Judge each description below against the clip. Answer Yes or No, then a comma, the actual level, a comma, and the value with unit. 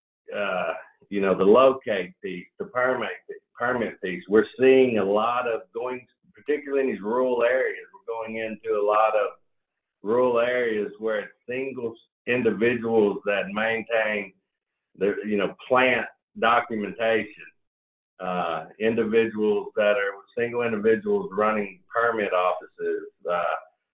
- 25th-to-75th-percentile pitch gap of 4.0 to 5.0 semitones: No, average, 3.2 semitones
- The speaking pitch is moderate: No, low, 115 Hz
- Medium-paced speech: No, slow, 130 wpm